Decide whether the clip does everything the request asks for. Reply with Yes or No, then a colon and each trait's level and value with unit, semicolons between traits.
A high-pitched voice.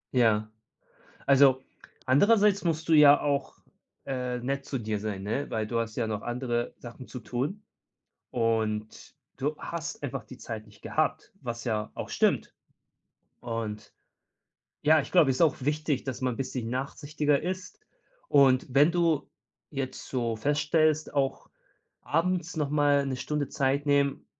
No: low, 135 Hz